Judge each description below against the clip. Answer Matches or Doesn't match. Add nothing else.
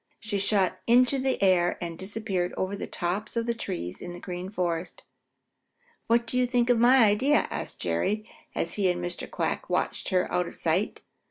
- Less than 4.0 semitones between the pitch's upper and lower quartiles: Doesn't match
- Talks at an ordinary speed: Matches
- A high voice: Matches